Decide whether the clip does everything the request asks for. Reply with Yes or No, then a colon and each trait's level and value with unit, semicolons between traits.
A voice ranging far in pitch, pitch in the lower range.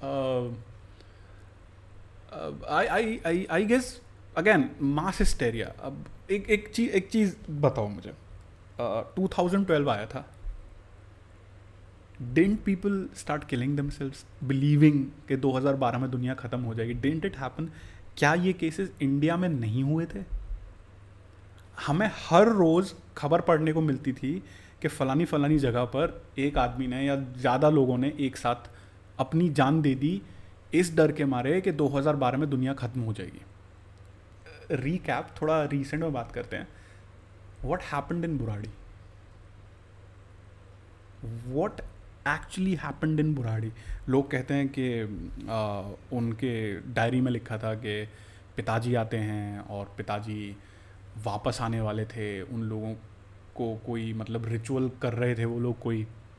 Yes: wide, 6.6 semitones; low, 120 Hz